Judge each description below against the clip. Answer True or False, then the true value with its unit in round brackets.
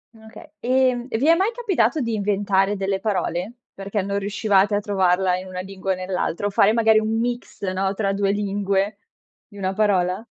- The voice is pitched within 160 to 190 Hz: False (205 Hz)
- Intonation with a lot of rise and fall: False (2.4 semitones)